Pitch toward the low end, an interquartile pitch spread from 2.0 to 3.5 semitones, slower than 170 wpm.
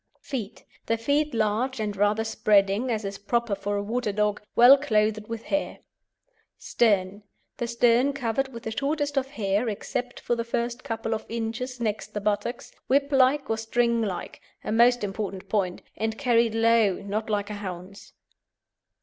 No: high, 225 Hz; average, 2.9 semitones; average, 160 wpm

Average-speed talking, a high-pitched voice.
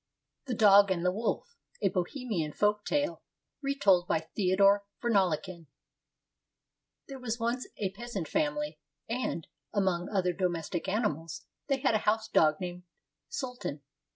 No: slow, 130 wpm; high, 200 Hz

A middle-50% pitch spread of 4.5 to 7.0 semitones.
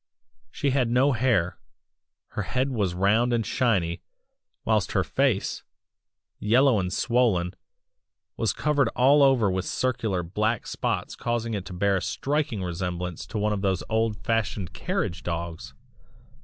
Yes: average, 5.0 semitones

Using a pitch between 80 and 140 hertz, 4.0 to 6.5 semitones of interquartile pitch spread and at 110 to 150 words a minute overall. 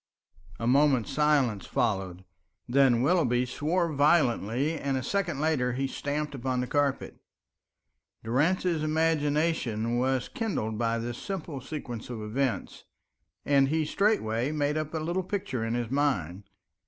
Yes: low, 135 Hz; average, 4.5 semitones; slow, 135 wpm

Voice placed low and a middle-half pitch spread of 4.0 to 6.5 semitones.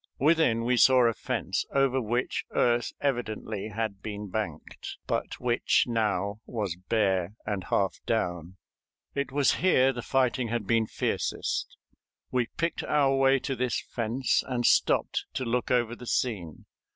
No: low, 120 Hz; average, 3.5 semitones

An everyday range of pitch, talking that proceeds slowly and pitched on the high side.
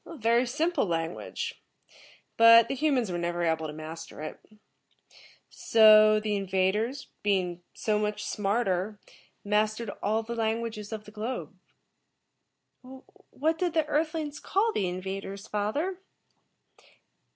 Yes: average, 4.8 semitones; slow, 125 wpm; high, 215 Hz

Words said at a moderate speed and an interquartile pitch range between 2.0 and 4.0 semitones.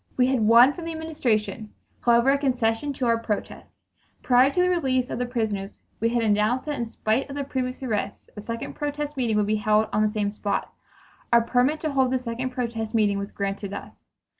No: fast, 215 wpm; average, 3.6 semitones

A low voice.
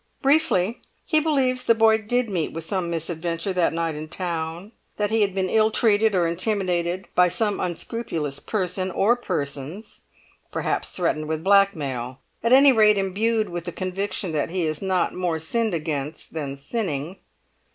No: medium, 185 Hz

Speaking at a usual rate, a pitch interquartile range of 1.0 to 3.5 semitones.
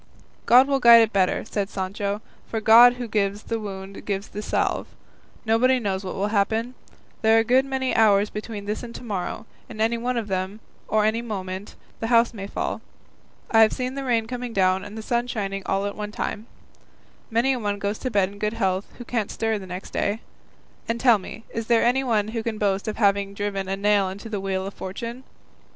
No: fast, 215 wpm; average, 2.8 semitones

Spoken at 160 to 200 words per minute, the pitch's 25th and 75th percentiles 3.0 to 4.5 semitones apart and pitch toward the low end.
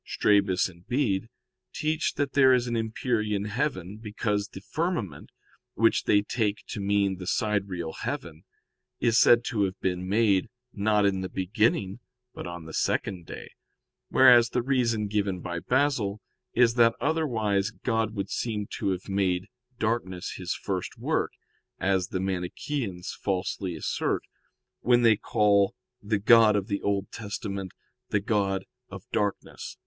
No: average, 145 wpm; average, 3.3 semitones; low, 105 Hz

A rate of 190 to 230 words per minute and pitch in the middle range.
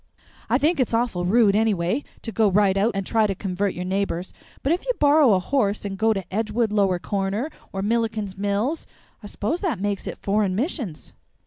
No: average, 200 wpm; high, 205 Hz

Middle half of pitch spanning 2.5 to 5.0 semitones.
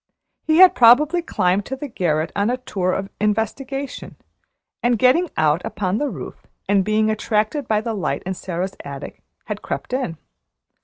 No: wide, 5.6 semitones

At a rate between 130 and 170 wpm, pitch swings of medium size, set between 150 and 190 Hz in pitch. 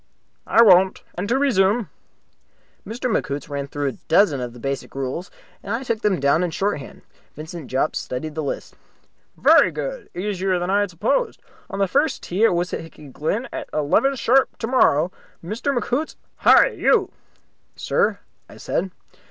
No: average, 160 wpm; wide, 7.1 semitones; medium, 185 Hz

